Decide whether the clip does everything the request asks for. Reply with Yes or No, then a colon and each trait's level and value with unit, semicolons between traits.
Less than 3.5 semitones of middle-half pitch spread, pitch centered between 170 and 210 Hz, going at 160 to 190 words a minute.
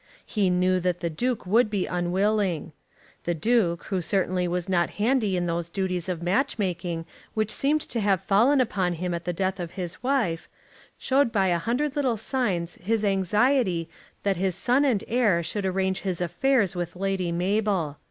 No: average, 3.9 semitones; high, 190 Hz; average, 180 wpm